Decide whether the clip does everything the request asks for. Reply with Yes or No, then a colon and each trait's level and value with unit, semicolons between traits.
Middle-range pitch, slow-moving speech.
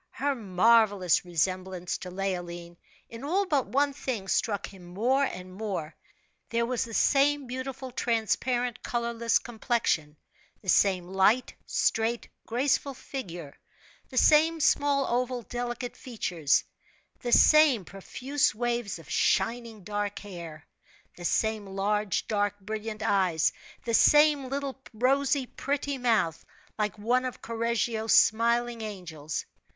No: high, 225 Hz; slow, 125 wpm